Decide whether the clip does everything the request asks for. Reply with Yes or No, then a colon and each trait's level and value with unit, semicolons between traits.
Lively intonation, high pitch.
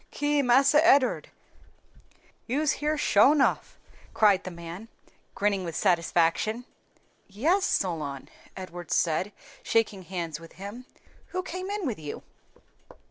Yes: wide, 8.6 semitones; high, 205 Hz